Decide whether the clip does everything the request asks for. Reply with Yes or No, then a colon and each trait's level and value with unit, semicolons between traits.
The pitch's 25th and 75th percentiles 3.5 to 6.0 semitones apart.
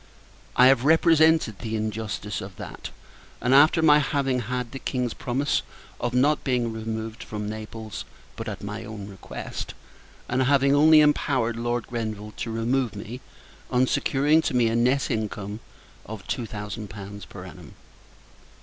Yes: average, 3.8 semitones